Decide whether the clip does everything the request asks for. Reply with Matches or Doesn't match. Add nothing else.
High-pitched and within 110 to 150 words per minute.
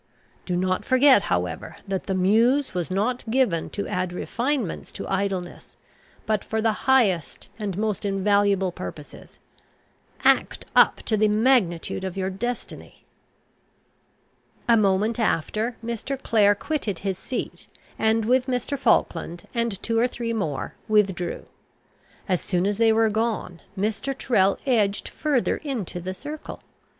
Matches